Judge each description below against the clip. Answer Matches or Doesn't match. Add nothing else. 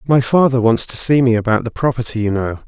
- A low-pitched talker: Matches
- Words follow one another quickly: Matches